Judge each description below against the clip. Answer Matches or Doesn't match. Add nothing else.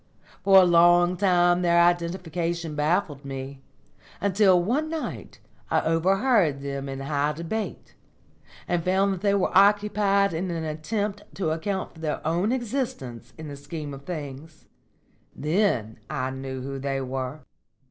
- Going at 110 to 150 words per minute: Matches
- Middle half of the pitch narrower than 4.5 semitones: Doesn't match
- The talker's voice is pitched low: Doesn't match